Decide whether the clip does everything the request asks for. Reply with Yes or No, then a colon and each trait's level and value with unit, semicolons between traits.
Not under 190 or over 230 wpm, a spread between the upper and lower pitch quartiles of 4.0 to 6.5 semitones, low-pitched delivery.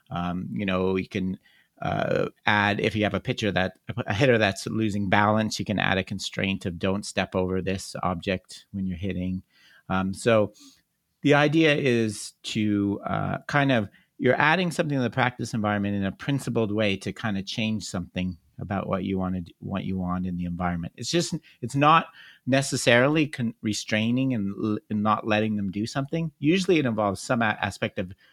Yes: average, 195 wpm; average, 4.7 semitones; low, 105 Hz